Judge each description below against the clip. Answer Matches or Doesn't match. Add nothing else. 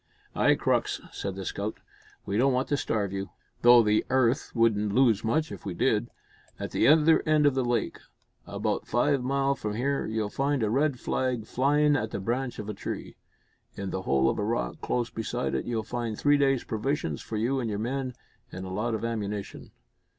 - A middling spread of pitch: Matches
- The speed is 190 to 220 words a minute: Matches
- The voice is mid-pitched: Doesn't match